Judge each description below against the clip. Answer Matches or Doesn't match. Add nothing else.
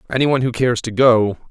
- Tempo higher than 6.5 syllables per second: Matches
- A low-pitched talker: Matches